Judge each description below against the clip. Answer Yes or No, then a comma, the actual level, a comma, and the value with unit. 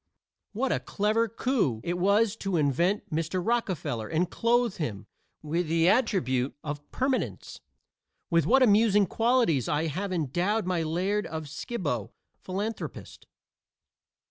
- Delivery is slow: Yes, slow, 125 wpm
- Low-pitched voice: No, medium, 185 Hz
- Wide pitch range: Yes, wide, 6.1 semitones